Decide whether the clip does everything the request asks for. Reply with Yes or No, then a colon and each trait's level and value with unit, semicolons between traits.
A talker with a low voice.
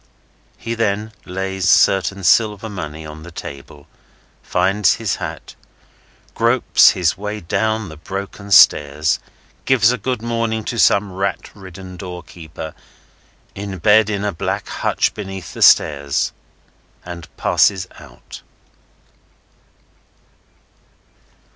Yes: very low, 95 Hz